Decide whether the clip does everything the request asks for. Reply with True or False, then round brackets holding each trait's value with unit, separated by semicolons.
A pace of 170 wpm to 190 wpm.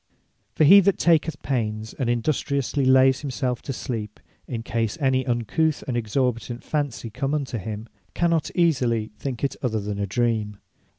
False (160 wpm)